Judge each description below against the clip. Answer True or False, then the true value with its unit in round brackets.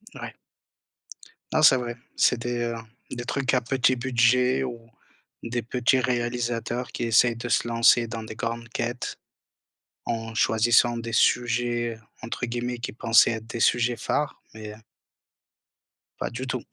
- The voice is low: True (120 Hz)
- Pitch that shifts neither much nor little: False (1.1 semitones)